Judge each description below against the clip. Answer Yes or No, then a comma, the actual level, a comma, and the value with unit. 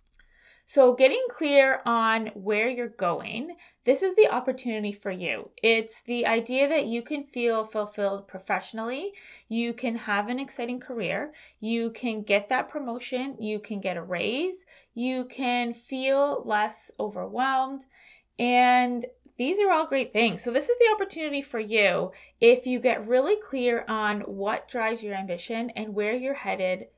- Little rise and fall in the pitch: No, average, 3.6 semitones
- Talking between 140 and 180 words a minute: Yes, average, 155 wpm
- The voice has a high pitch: Yes, high, 240 Hz